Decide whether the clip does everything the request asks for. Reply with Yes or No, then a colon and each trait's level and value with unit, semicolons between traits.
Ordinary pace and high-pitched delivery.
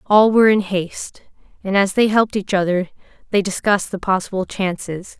Yes: average, 175 wpm; high, 195 Hz